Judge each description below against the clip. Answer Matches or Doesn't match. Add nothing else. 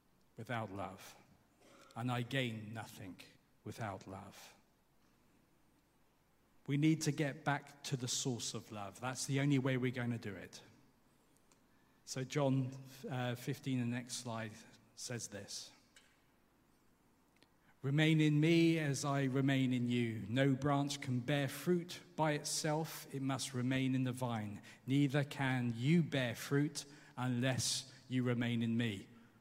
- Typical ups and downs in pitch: Matches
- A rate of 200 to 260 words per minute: Doesn't match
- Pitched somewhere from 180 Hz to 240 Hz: Doesn't match